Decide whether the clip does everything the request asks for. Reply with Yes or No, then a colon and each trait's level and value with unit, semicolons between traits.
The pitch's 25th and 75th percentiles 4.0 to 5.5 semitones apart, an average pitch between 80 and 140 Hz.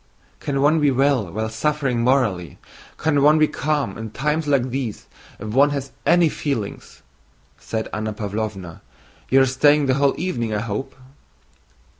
Yes: average, 4.9 semitones; low, 135 Hz